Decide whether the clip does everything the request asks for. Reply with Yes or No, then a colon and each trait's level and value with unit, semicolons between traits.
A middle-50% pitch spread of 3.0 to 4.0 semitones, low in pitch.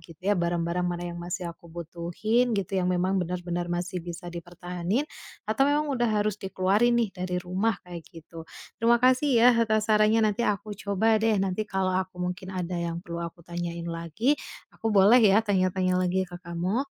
No: average, 3.7 semitones; medium, 185 Hz